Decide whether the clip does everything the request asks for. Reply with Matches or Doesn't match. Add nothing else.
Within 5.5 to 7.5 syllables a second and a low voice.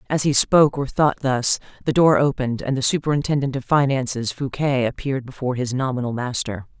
Matches